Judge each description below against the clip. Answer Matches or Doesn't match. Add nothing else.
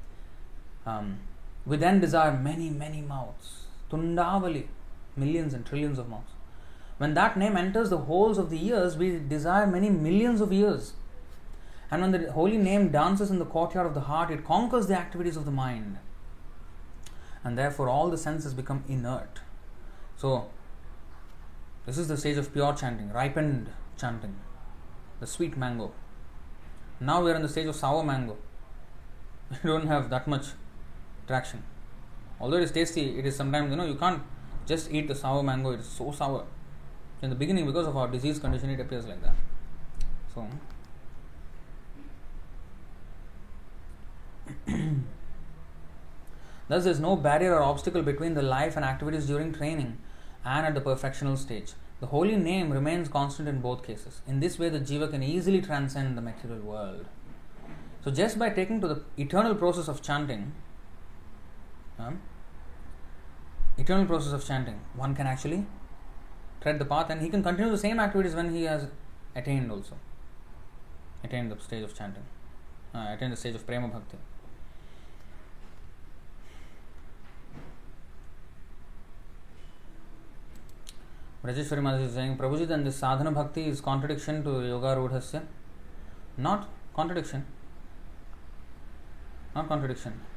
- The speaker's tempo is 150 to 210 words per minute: Doesn't match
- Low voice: Matches